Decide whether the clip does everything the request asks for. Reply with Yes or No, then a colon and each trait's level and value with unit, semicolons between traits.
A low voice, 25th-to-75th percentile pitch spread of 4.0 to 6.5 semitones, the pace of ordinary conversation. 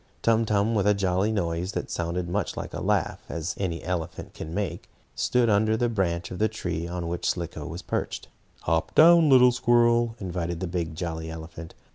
Yes: very low, 90 Hz; average, 4.6 semitones; average, 195 wpm